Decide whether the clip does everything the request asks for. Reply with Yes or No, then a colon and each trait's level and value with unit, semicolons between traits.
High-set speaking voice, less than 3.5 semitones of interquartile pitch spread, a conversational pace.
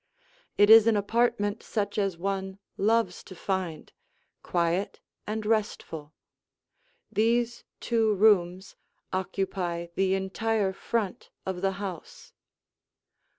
No: high, 195 Hz; average, 2.7 semitones; slow, 105 wpm